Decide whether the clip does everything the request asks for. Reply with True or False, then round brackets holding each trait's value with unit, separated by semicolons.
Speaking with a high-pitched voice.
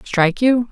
True (220 Hz)